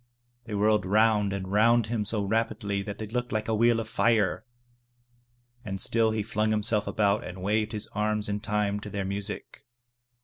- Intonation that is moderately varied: No, narrow, 1.5 semitones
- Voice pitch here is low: Yes, low, 105 Hz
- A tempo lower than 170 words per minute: No, average, 180 wpm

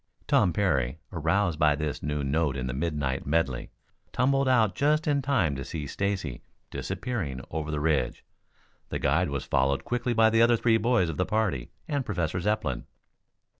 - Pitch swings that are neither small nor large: No, wide, 7.8 semitones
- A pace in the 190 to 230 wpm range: No, average, 170 wpm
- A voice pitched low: Yes, very low, 85 Hz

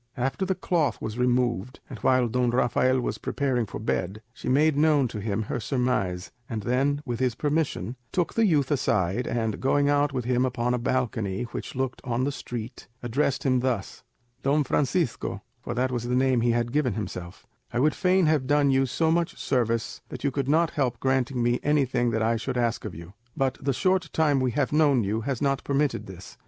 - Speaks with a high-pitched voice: No, low, 130 Hz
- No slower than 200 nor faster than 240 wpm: Yes, fast, 205 wpm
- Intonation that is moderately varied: Yes, average, 3.3 semitones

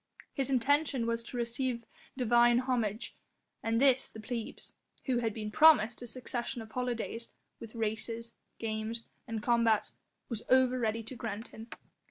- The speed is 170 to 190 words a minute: No, average, 150 wpm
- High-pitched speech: Yes, high, 235 Hz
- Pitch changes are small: Yes, narrow, 2.0 semitones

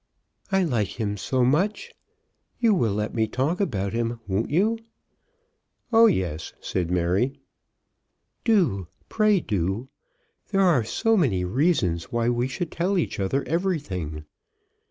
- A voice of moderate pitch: No, low, 125 Hz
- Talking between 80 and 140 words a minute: Yes, slow, 135 wpm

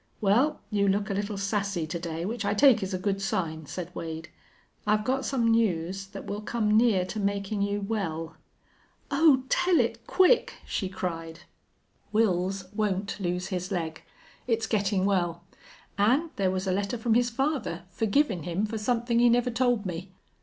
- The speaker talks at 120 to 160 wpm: No, average, 175 wpm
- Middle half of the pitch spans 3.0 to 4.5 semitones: Yes, average, 3.9 semitones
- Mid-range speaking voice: No, high, 200 Hz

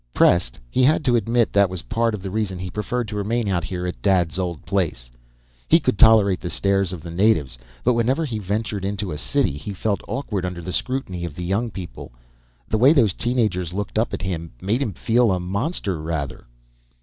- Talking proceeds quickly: Yes, fast, 220 wpm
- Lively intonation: No, average, 4.2 semitones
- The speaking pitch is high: No, low, 100 Hz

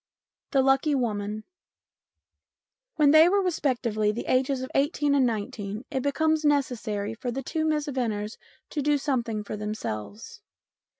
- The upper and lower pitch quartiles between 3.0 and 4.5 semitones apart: No, average, 5.2 semitones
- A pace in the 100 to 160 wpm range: Yes, average, 155 wpm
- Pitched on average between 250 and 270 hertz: Yes, very high, 260 Hz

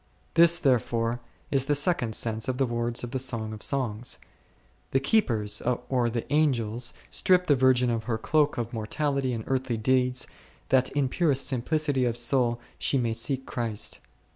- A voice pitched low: Yes, low, 125 Hz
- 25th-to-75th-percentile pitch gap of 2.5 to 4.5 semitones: Yes, average, 2.9 semitones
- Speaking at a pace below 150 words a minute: No, average, 165 wpm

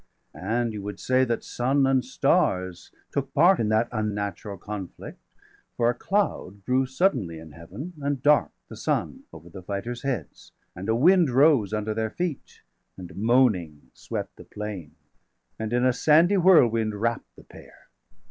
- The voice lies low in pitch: Yes, low, 115 Hz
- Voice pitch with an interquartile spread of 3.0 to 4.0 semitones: No, average, 5.0 semitones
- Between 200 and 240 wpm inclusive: No, average, 165 wpm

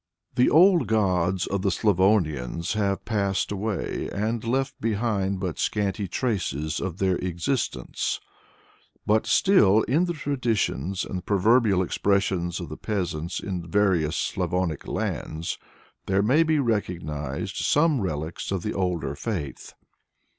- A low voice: Yes, low, 100 Hz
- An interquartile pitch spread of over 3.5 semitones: Yes, average, 4.2 semitones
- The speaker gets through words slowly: Yes, slow, 125 wpm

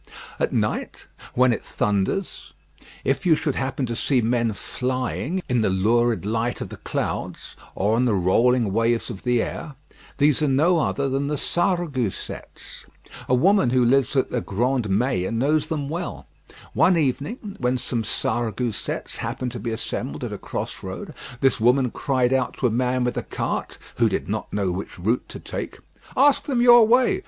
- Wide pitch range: No, average, 4.1 semitones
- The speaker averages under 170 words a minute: No, average, 175 wpm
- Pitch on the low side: Yes, low, 125 Hz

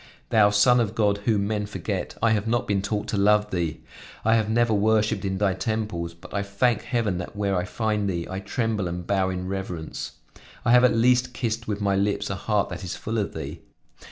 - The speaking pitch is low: Yes, low, 105 Hz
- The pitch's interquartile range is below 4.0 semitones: Yes, narrow, 2.5 semitones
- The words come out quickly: Yes, fast, 220 wpm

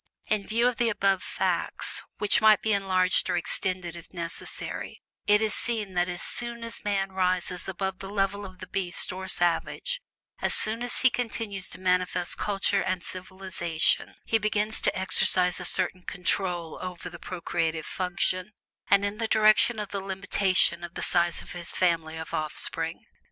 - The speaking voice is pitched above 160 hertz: Yes, high, 190 Hz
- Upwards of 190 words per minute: No, average, 170 wpm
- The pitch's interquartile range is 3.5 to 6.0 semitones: No, average, 2.7 semitones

